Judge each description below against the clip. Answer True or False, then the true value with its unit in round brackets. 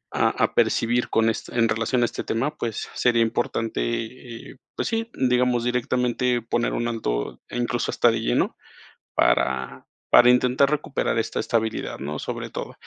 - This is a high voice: False (120 Hz)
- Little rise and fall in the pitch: True (1.7 semitones)